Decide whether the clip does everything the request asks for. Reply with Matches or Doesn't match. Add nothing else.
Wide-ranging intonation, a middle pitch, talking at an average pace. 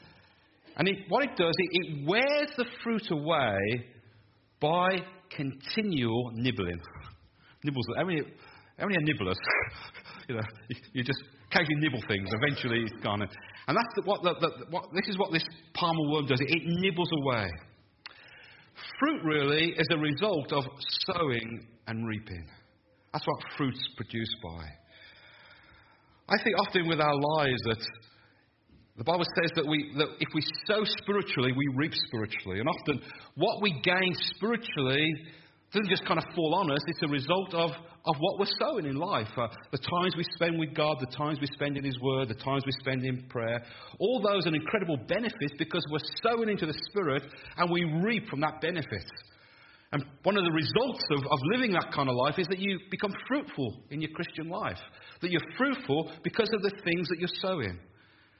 Matches